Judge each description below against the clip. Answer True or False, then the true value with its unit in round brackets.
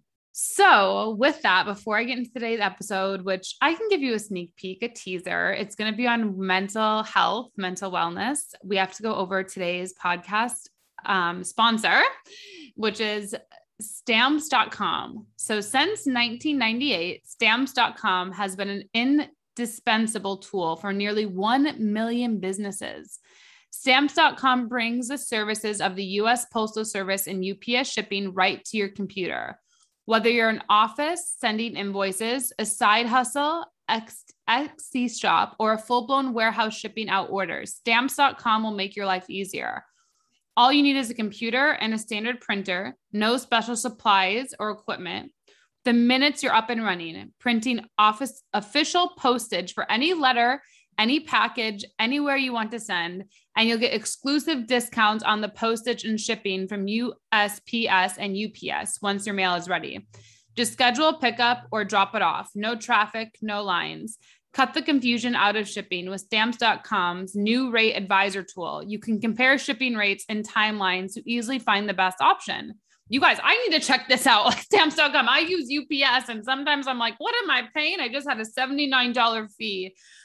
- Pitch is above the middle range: True (225 Hz)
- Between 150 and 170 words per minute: True (160 wpm)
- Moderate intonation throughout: True (4.3 semitones)